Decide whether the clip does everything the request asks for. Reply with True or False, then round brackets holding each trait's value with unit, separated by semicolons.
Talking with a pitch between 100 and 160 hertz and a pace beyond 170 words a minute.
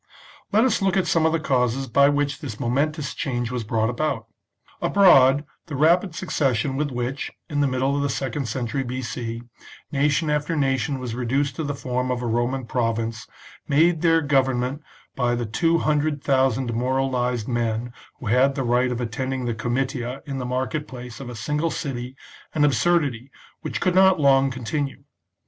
True (135 Hz; 180 wpm)